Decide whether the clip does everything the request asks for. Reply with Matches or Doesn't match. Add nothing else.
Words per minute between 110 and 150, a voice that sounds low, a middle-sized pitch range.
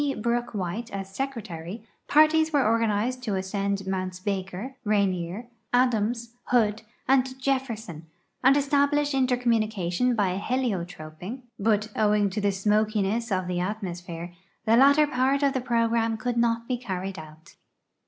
Doesn't match